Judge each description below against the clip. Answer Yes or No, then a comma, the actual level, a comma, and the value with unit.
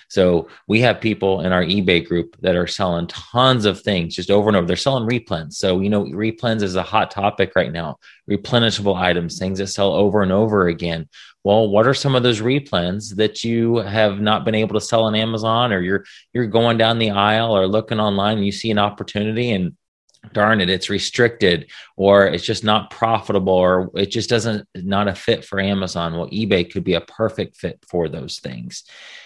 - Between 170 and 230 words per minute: Yes, fast, 205 wpm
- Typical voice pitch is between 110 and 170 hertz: No, low, 100 Hz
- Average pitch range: Yes, average, 3.1 semitones